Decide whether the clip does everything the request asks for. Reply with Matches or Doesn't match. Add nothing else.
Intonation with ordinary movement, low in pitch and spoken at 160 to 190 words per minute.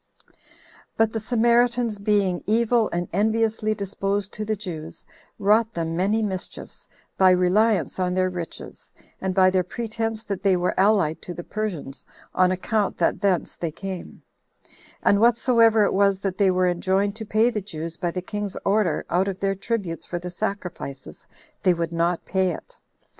Doesn't match